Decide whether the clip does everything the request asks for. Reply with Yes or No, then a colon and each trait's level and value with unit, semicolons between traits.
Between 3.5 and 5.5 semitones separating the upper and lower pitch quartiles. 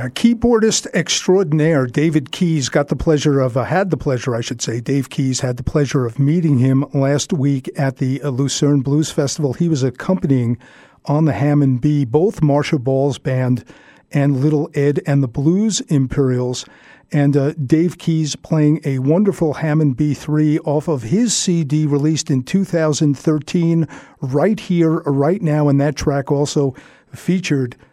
No: average, 2.8 semitones